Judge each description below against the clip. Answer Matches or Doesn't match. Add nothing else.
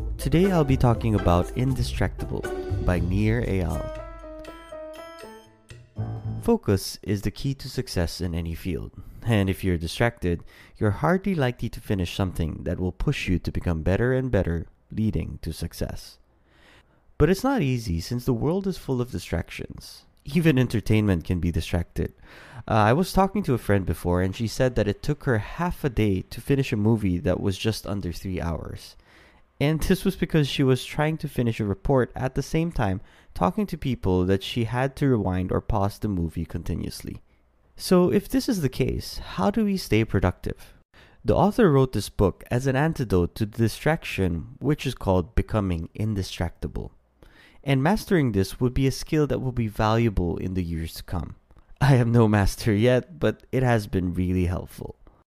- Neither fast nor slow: Matches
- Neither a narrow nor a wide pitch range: Doesn't match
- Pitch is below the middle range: Matches